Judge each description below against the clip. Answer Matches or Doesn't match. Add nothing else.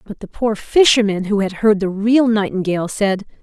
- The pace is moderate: Matches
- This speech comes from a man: Doesn't match